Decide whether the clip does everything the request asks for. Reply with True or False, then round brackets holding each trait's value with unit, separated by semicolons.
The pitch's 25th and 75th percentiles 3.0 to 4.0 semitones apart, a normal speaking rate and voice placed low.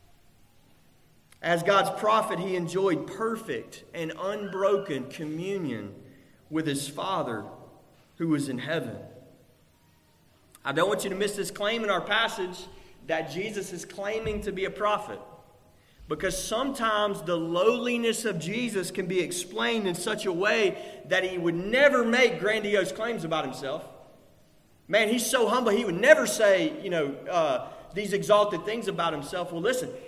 False (3.7 semitones; 150 wpm; 195 Hz)